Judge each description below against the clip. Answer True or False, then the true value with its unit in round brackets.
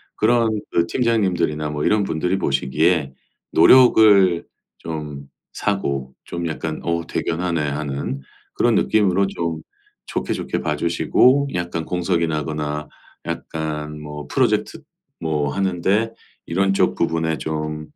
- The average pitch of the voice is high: False (85 Hz)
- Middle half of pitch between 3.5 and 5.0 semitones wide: True (4.1 semitones)